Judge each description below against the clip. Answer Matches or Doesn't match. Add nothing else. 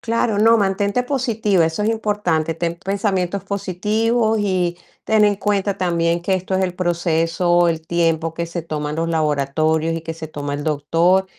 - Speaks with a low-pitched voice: Doesn't match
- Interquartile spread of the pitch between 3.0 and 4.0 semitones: Matches